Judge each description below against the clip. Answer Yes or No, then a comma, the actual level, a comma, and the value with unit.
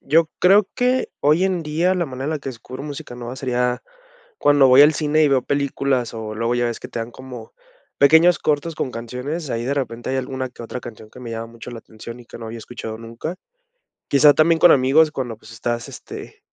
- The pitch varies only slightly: No, average, 4.4 semitones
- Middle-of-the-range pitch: No, low, 130 Hz